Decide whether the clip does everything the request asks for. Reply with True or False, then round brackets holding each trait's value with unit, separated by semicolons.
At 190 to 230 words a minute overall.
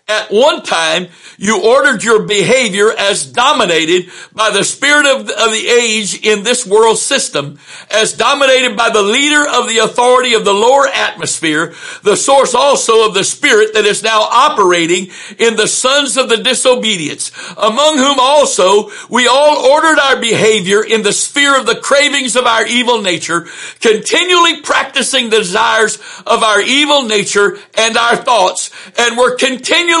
False (160 wpm)